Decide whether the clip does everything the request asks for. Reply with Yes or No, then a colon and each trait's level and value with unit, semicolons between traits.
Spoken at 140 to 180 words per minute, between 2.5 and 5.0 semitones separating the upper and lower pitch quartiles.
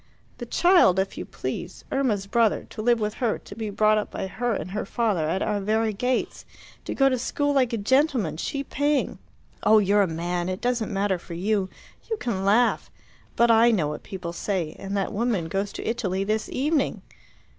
No: average, 200 wpm; average, 3.9 semitones